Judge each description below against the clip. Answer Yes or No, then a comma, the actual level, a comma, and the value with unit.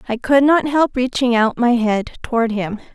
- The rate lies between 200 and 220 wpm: Yes, fast, 205 wpm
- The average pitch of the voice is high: Yes, high, 245 Hz